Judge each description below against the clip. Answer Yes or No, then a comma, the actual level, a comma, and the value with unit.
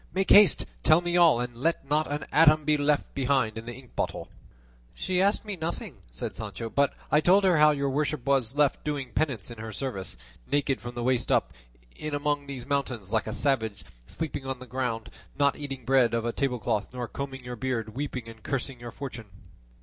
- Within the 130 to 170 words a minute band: No, fast, 205 wpm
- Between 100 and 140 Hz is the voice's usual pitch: Yes, low, 135 Hz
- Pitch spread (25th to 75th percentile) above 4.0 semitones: No, average, 3.7 semitones